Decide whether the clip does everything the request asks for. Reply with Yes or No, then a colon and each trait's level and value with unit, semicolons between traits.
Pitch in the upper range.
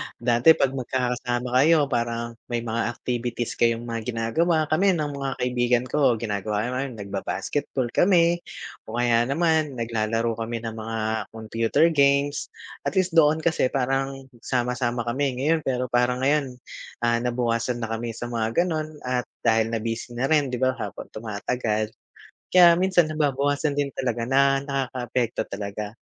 No: low, 125 Hz